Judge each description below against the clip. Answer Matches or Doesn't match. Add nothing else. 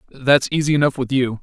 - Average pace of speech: Doesn't match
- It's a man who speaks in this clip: Matches